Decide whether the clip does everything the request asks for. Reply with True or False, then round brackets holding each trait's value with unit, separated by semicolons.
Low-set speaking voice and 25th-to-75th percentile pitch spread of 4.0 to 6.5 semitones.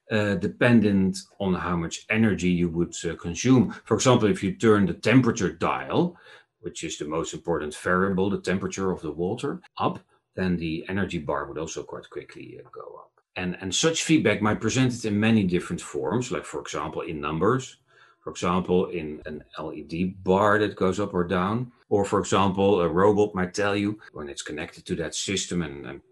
False (95 Hz; 3.1 semitones)